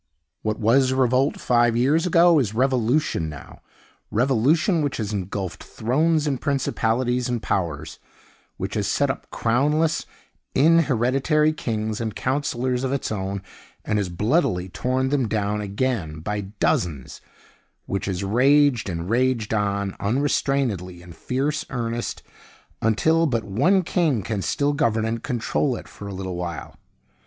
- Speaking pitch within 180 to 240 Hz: No, low, 120 Hz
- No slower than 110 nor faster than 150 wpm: Yes, average, 140 wpm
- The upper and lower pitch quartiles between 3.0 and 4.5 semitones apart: No, average, 5.3 semitones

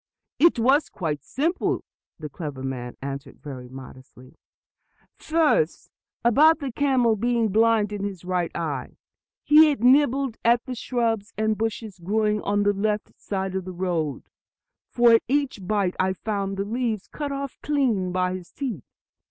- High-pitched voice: Yes, high, 210 Hz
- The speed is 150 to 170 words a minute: Yes, average, 155 wpm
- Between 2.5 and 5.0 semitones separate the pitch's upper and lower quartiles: No, wide, 5.5 semitones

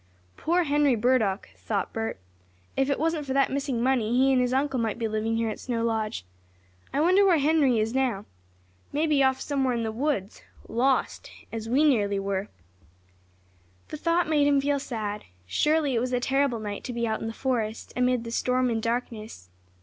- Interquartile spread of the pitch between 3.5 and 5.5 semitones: Yes, average, 4.0 semitones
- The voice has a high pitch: Yes, very high, 250 Hz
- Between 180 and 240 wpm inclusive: Yes, average, 190 wpm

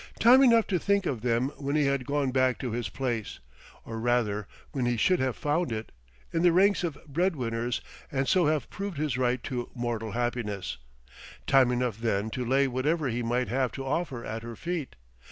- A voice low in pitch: Yes, low, 130 Hz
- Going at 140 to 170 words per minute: No, average, 200 wpm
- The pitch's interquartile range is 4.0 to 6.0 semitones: Yes, average, 4.3 semitones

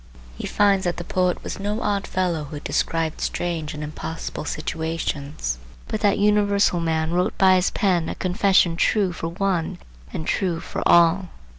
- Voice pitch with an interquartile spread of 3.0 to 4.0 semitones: Yes, average, 3.3 semitones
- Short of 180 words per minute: Yes, average, 165 wpm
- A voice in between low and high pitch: Yes, medium, 175 Hz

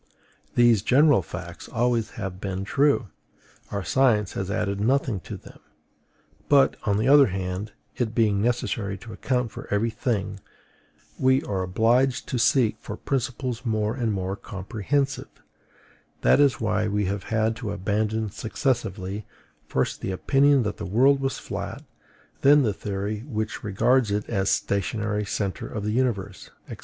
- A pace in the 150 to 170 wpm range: Yes, average, 155 wpm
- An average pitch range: Yes, average, 3.7 semitones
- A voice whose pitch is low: Yes, low, 110 Hz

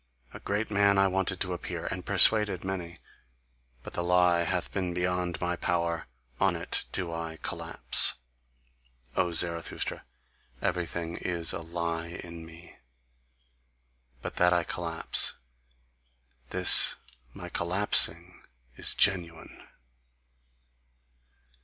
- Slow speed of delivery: Yes, slow, 110 wpm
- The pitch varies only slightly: Yes, narrow, 1.5 semitones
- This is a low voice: Yes, very low, 85 Hz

